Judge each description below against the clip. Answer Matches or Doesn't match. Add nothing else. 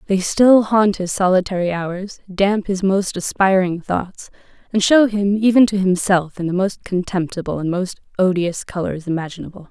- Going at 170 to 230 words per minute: Doesn't match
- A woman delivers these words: Matches